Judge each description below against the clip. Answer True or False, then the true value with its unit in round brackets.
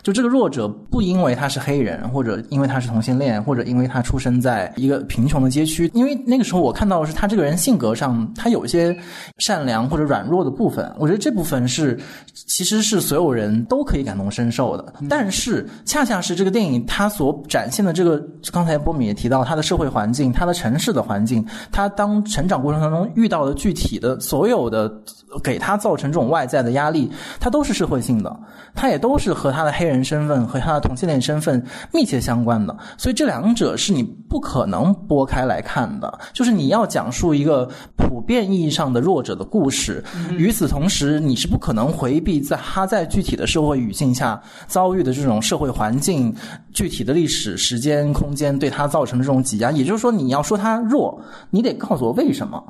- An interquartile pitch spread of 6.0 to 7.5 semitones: True (7.1 semitones)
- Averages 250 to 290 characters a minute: False (325 characters per minute)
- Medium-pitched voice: True (150 Hz)